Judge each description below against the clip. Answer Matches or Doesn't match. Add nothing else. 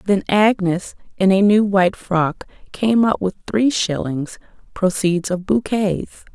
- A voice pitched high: Matches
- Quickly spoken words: Doesn't match